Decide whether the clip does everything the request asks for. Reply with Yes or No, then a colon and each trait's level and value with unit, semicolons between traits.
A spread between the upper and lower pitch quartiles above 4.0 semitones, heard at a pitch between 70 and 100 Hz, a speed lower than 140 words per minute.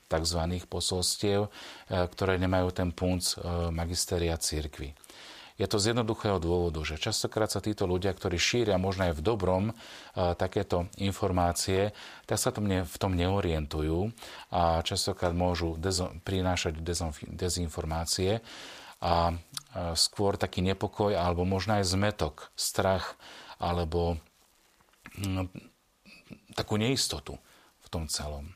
No: average, 2.7 semitones; very low, 90 Hz; slow, 110 wpm